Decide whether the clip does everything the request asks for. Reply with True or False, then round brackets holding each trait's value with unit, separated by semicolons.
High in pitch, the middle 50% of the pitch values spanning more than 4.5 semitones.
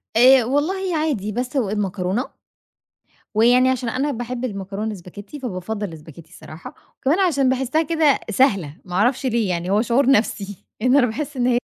True (240 Hz; 4.9 semitones)